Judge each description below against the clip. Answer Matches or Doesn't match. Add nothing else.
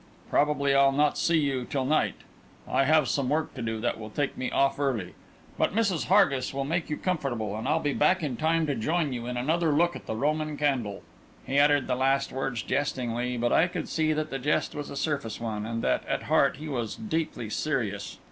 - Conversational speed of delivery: Doesn't match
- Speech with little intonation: Doesn't match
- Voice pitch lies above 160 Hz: Doesn't match